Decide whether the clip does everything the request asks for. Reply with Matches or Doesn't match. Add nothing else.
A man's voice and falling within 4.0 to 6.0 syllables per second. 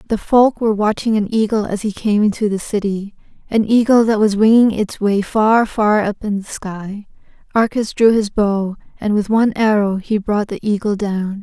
Doesn't match